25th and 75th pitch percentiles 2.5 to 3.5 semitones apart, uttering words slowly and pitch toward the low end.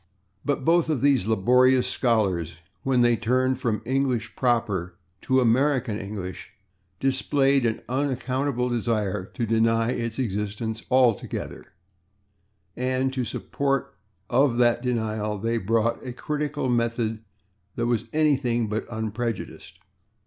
Yes: average, 2.8 semitones; slow, 120 wpm; low, 120 Hz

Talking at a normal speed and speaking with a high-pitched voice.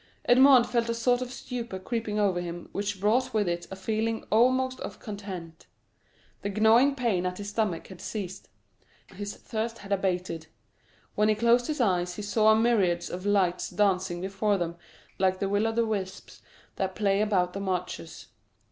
Yes: average, 175 wpm; high, 205 Hz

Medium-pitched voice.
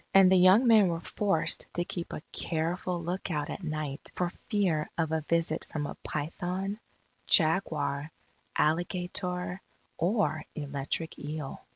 Yes: medium, 170 Hz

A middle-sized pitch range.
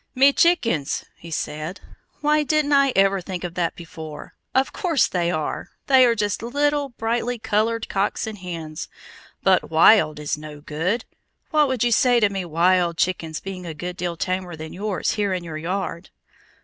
No: wide, 6.0 semitones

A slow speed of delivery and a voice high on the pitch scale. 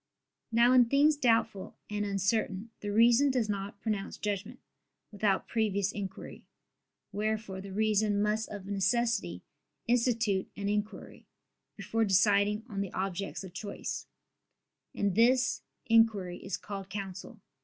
Yes: slow, 125 wpm; high, 210 Hz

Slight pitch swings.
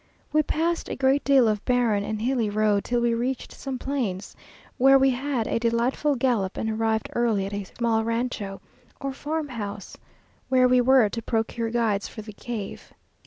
No: average, 3.5 semitones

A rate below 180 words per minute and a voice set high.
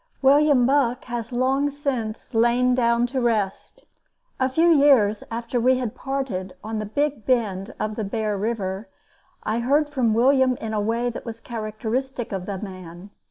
Yes: average, 165 wpm; high, 235 Hz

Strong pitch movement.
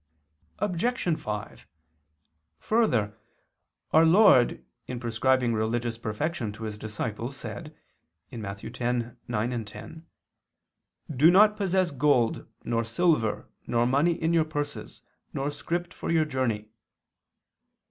Yes: wide, 6.4 semitones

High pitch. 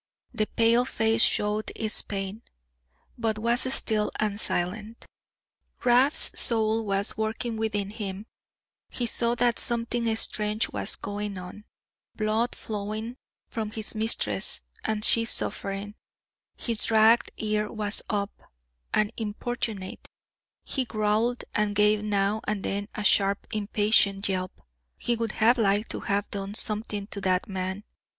Yes: high, 215 Hz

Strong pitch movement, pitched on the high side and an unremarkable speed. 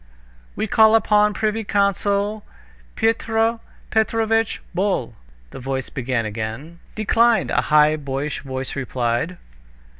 No: wide, 8.6 semitones; high, 200 Hz; slow, 115 wpm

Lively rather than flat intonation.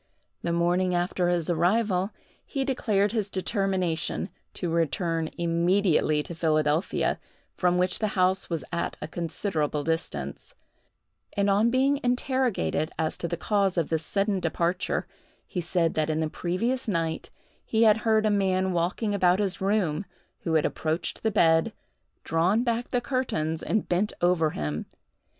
No: average, 4.0 semitones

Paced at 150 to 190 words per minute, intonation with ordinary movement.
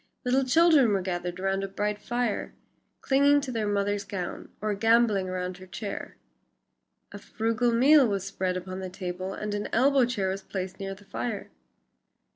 Yes: average, 170 wpm; average, 3.9 semitones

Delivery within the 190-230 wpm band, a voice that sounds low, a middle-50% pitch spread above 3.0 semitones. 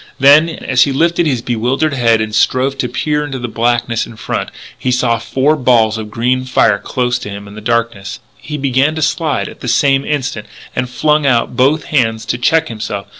Yes: average, 200 wpm; low, 125 Hz; average, 3.6 semitones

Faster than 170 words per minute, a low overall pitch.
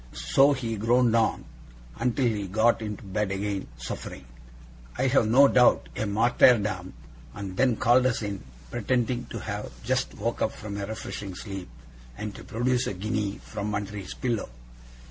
No: average, 165 wpm; low, 110 Hz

